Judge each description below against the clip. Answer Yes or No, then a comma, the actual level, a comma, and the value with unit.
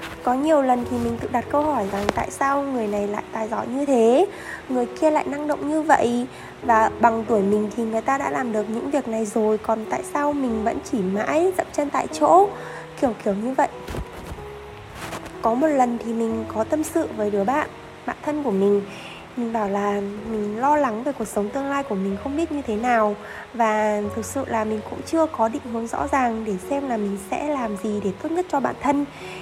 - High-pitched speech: Yes, high, 230 Hz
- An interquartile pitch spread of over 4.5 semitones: Yes, average, 5.1 semitones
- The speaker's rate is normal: Yes, average, 230 wpm